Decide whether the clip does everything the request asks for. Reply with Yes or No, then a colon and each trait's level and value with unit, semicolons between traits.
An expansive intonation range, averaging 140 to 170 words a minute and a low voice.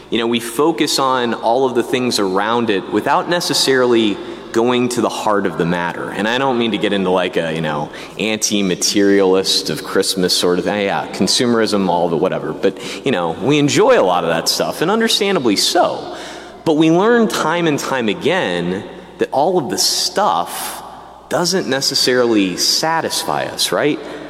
No: wide, 6.8 semitones; average, 180 wpm; low, 115 Hz